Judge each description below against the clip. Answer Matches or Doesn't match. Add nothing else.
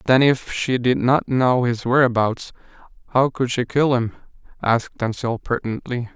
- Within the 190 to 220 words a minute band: Doesn't match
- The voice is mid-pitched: Doesn't match